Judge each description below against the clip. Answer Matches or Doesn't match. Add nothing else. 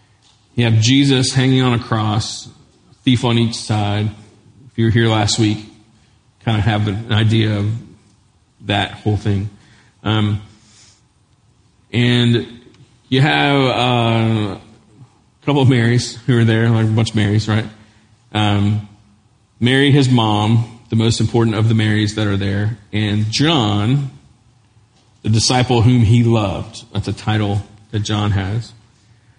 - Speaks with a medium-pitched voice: Doesn't match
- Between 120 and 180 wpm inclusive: Matches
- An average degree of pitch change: Doesn't match